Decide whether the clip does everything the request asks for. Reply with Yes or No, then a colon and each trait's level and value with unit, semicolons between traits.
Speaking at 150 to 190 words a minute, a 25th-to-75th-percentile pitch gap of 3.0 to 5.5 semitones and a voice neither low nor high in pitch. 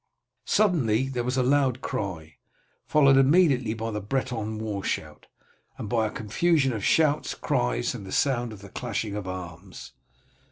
No: average, 160 wpm; average, 4.9 semitones; low, 115 Hz